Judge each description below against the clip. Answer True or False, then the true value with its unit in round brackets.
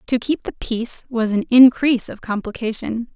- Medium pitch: False (235 Hz)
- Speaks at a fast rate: False (170 wpm)